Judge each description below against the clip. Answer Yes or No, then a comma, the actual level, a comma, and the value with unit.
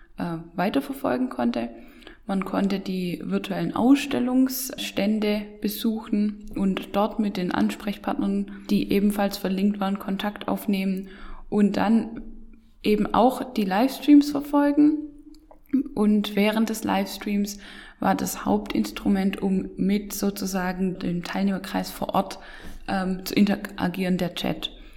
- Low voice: No, high, 205 Hz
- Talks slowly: Yes, slow, 110 wpm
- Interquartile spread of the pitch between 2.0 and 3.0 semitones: No, average, 3.5 semitones